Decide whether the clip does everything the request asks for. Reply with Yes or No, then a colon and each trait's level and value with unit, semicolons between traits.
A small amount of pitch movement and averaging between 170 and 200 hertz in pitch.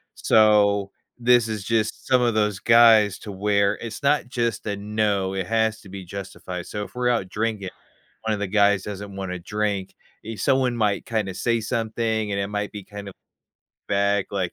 No: narrow, 2.2 semitones; low, 105 Hz